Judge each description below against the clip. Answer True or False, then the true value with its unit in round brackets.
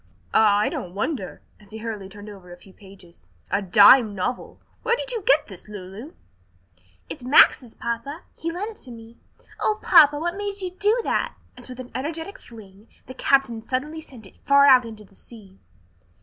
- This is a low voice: False (235 Hz)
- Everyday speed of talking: True (190 wpm)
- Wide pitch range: True (7.0 semitones)